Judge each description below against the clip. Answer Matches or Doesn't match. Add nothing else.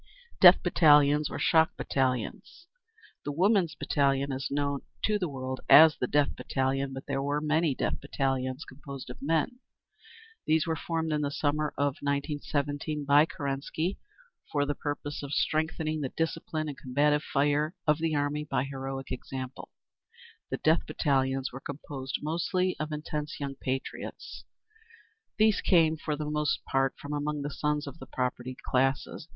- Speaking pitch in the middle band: Matches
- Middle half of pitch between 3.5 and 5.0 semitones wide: Doesn't match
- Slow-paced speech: Doesn't match